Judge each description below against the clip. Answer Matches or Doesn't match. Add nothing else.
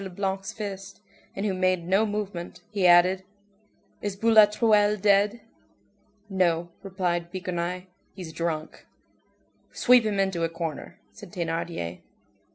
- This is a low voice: Doesn't match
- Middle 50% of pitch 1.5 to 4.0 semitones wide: Matches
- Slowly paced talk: Matches